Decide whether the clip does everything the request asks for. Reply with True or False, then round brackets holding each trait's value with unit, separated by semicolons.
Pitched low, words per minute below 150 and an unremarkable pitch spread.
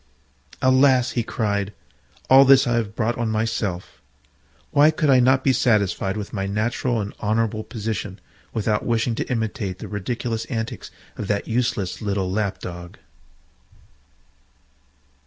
True (110 Hz; 140 wpm; 3.1 semitones)